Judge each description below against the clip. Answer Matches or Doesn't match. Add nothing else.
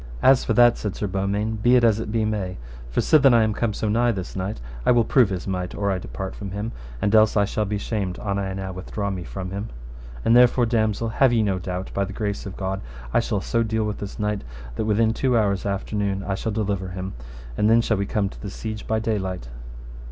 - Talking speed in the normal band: Doesn't match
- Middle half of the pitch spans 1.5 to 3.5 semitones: Matches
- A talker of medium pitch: Doesn't match